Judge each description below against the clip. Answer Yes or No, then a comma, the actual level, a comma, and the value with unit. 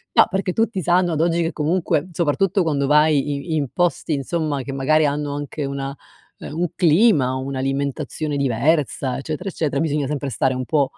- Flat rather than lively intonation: No, average, 3.2 semitones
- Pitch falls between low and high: Yes, medium, 150 Hz